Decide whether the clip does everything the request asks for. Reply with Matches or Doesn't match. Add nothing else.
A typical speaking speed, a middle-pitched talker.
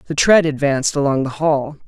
Matches